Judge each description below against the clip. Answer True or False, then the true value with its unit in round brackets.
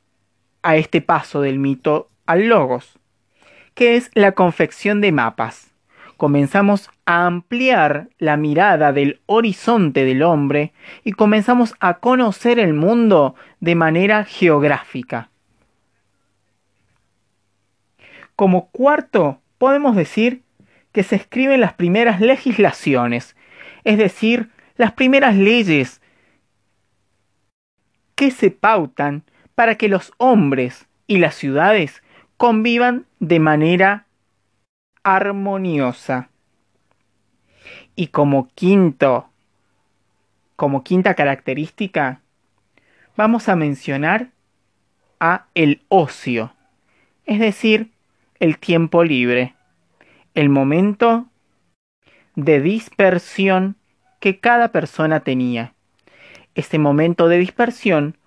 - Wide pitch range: True (8.2 semitones)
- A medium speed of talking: False (90 wpm)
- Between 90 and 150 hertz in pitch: False (170 Hz)